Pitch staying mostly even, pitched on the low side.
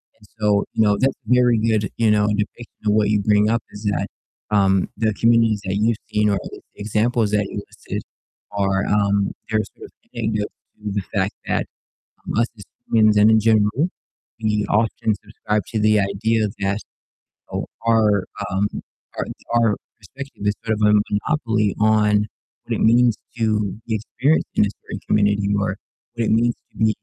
Yes: narrow, 1.5 semitones; low, 105 Hz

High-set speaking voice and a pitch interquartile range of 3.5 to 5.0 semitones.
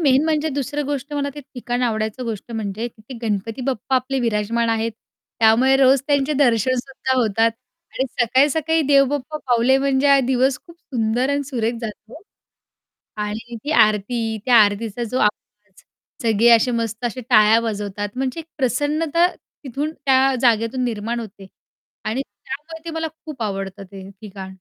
Yes: high, 245 Hz; average, 3.9 semitones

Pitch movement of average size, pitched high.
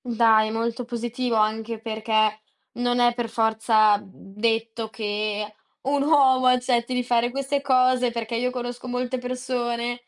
No: narrow, 2.1 semitones; high, 235 Hz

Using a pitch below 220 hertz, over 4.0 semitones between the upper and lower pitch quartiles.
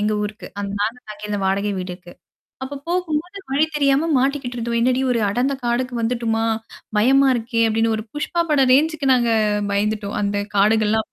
No: high, 235 Hz; average, 4.4 semitones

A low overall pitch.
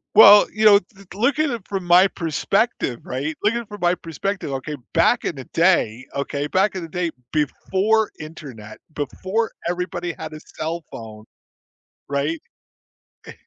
No: medium, 175 Hz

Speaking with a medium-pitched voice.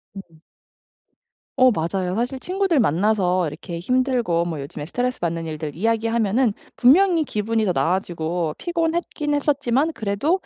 No: high, 215 Hz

